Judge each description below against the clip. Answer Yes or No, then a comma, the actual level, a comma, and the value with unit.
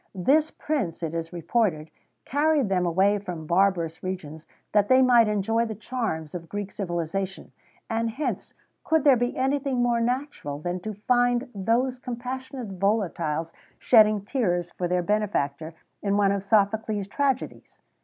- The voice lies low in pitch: No, high, 205 Hz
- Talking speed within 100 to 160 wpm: Yes, average, 155 wpm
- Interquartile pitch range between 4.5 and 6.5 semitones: Yes, wide, 5.6 semitones